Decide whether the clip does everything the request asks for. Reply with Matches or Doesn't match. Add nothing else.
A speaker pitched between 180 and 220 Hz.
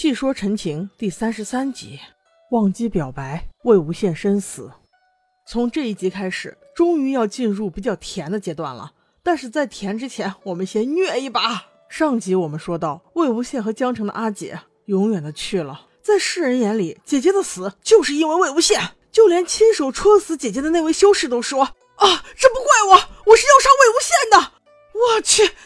Doesn't match